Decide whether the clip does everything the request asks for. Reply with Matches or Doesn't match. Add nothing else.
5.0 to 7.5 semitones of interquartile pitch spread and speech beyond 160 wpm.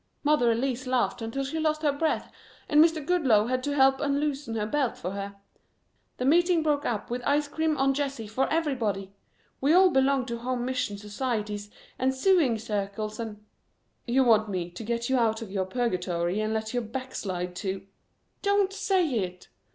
Matches